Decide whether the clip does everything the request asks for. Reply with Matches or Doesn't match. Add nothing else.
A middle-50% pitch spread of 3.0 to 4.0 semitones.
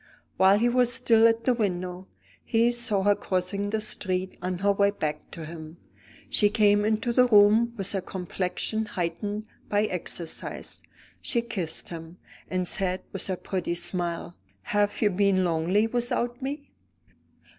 Matches